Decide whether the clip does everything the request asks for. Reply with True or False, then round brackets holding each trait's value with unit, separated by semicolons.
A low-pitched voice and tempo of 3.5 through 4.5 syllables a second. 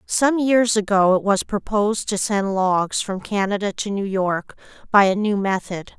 False (200 Hz; 4.4 syllables/s)